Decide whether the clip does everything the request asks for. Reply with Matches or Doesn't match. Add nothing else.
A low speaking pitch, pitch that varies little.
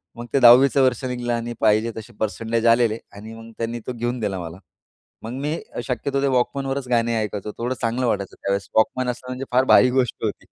Matches